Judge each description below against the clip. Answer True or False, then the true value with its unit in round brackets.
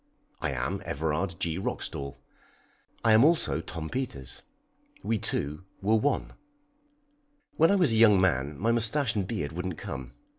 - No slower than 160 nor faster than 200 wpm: False (150 wpm)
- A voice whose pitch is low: True (95 Hz)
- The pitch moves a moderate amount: False (7.1 semitones)